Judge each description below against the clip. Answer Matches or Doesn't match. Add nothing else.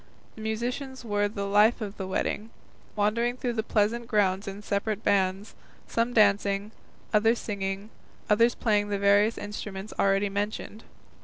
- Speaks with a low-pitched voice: Doesn't match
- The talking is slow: Doesn't match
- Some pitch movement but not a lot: Doesn't match